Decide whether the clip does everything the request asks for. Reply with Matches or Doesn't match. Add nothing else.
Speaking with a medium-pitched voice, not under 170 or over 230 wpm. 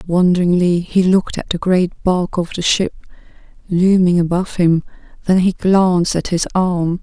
Doesn't match